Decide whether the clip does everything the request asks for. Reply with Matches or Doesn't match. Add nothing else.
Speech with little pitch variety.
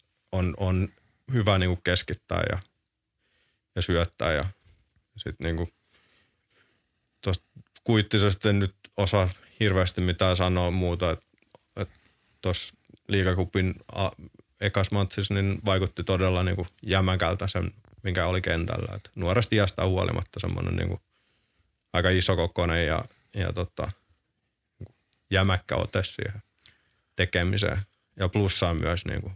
Matches